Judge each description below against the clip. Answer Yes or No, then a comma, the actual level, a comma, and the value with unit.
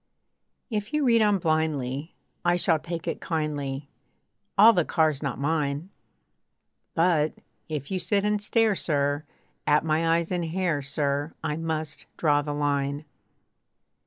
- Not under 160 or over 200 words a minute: No, average, 140 wpm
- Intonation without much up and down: No, average, 3.4 semitones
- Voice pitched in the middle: Yes, medium, 160 Hz